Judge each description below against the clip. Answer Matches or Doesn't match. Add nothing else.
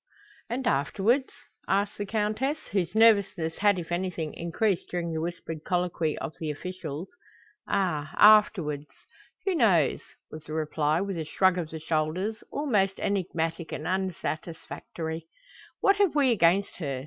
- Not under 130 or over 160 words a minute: Matches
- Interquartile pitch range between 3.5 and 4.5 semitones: Matches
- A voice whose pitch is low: Doesn't match